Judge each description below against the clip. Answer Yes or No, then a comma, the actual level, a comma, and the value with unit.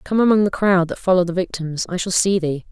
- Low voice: No, medium, 185 Hz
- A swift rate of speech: Yes, fast, 245 wpm